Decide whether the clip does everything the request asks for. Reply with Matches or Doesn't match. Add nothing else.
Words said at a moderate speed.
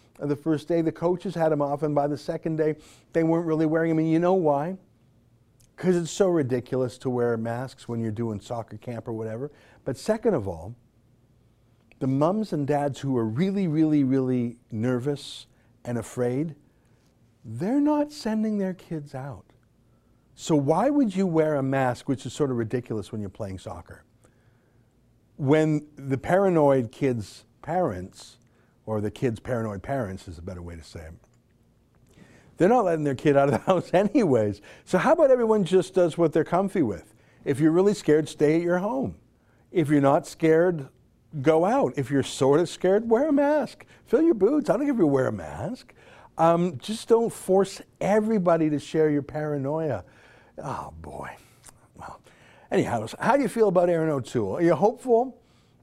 Matches